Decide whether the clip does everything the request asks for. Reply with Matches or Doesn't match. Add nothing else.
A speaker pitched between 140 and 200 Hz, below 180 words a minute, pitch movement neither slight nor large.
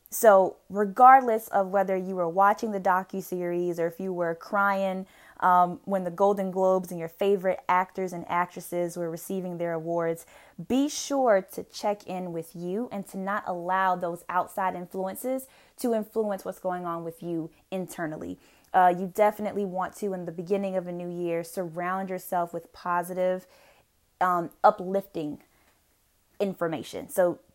Doesn't match